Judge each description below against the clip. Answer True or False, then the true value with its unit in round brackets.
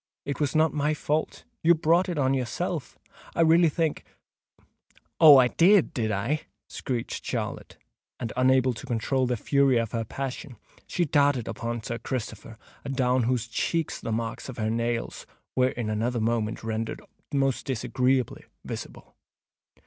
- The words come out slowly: False (145 wpm)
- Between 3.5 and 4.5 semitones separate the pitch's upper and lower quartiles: True (3.9 semitones)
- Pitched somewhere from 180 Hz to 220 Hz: False (130 Hz)